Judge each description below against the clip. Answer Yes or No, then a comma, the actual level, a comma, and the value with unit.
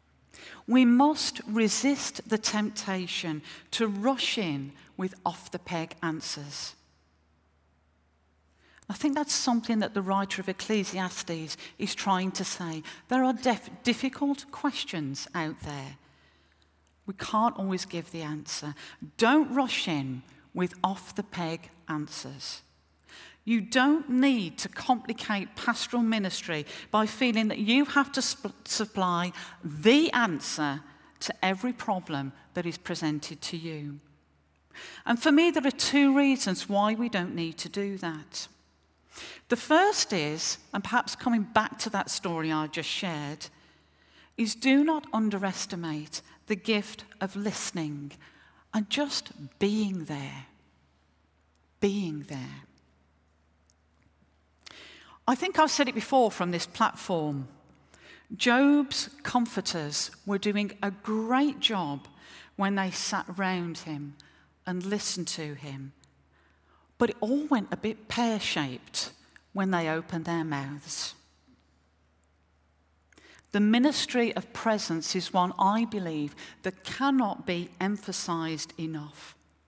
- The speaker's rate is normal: No, slow, 125 wpm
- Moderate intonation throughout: No, wide, 7.4 semitones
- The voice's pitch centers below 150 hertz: No, medium, 185 Hz